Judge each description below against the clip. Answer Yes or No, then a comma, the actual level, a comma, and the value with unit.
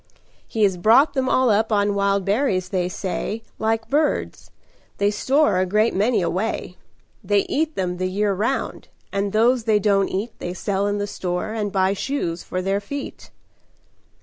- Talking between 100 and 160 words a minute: No, average, 175 wpm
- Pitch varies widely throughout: No, average, 2.9 semitones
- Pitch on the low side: No, high, 205 Hz